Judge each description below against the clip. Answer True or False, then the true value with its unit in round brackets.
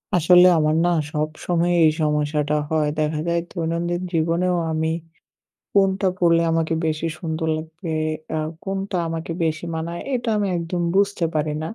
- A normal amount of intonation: False (2.0 semitones)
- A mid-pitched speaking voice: True (165 Hz)